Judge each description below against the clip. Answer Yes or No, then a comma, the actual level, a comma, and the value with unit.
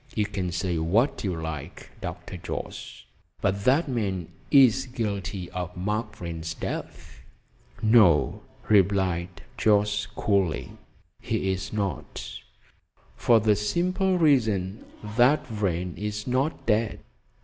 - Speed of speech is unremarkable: No, slow, 110 wpm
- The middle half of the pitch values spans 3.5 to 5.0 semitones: Yes, average, 4.0 semitones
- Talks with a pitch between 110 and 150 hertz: No, low, 100 Hz